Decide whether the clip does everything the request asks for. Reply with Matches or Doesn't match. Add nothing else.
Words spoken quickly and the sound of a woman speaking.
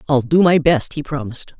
Matches